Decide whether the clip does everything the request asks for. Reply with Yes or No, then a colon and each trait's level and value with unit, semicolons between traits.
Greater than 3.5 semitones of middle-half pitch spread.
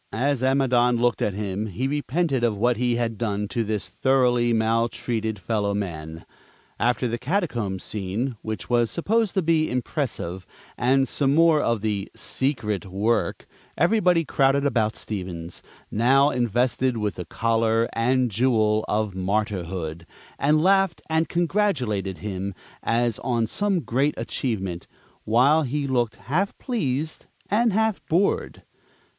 Yes: average, 4.8 semitones